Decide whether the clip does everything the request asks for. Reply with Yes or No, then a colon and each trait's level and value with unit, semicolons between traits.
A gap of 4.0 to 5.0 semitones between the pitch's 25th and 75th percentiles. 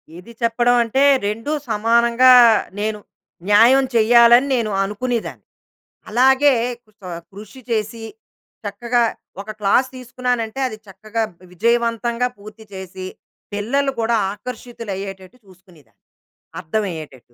No: average, 3.1 semitones